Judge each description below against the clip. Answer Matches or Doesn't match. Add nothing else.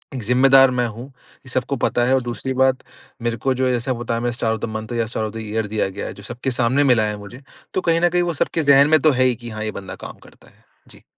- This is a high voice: Doesn't match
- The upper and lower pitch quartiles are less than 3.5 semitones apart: Matches